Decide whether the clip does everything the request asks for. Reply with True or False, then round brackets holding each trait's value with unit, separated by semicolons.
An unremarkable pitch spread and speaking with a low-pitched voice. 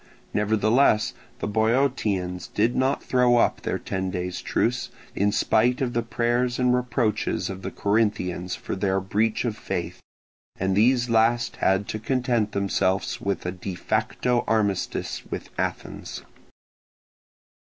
True (3.9 semitones; 110 Hz)